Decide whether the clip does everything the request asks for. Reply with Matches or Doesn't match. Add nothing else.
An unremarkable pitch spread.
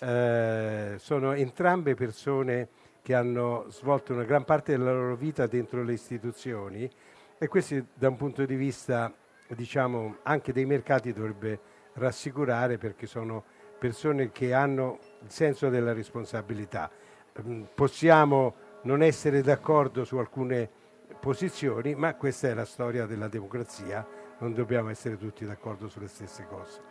Matches